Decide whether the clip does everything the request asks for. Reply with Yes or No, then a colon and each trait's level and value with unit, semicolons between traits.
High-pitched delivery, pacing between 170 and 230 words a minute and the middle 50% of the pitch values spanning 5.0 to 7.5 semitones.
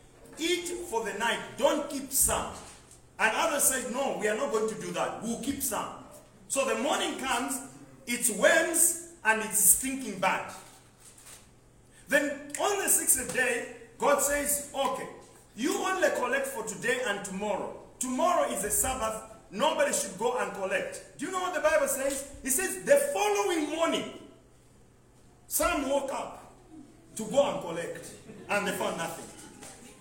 No: very high, 275 Hz; average, 155 wpm; wide, 5.5 semitones